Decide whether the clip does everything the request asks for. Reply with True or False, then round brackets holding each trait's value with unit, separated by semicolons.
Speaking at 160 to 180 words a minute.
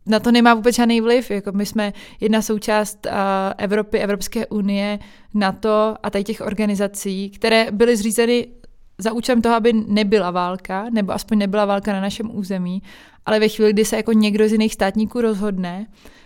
True (170 wpm)